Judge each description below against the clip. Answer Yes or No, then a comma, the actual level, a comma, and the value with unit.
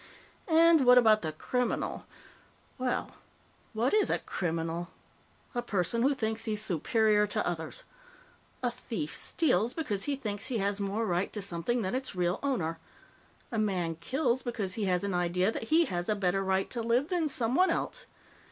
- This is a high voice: Yes, high, 215 Hz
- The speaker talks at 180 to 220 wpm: No, average, 170 wpm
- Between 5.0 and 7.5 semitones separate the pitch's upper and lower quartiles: Yes, wide, 5.4 semitones